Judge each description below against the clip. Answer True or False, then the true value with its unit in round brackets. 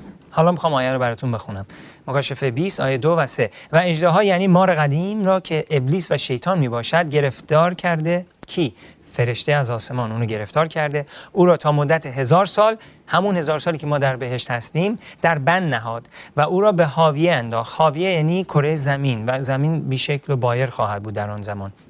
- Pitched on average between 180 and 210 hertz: False (150 Hz)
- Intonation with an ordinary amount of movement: True (4.9 semitones)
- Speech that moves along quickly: True (190 wpm)